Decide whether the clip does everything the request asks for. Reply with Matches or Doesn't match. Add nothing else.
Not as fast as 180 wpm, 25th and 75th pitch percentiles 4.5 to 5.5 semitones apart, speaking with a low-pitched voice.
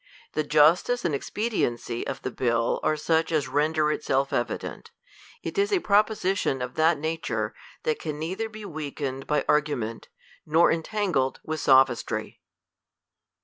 Doesn't match